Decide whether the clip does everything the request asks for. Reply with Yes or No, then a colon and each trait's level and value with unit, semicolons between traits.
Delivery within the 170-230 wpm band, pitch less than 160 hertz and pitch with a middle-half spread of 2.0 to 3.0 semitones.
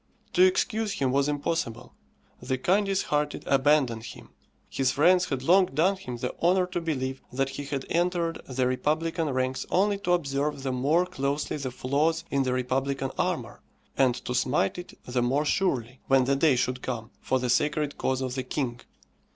No: average, 180 wpm; medium, 140 Hz; average, 4.3 semitones